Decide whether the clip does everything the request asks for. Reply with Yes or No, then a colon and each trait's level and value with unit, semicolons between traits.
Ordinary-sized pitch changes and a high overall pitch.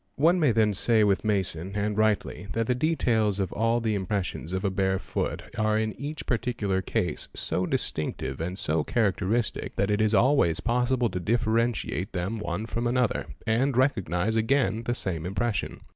No: average, 3.8 semitones; low, 110 Hz